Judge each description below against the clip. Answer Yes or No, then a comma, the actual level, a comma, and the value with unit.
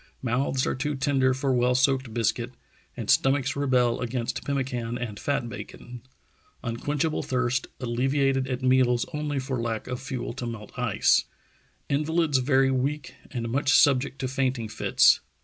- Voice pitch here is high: No, low, 130 Hz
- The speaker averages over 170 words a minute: No, average, 150 wpm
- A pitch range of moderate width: No, narrow, 2.1 semitones